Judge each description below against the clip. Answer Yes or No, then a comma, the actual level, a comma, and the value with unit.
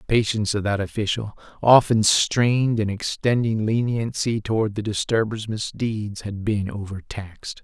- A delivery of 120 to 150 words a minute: Yes, slow, 135 wpm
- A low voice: Yes, low, 110 Hz